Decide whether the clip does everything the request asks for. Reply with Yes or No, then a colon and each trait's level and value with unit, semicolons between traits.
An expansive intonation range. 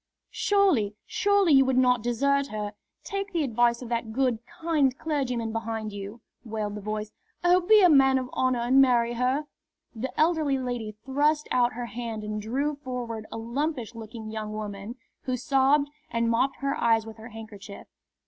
No: average, 3.9 semitones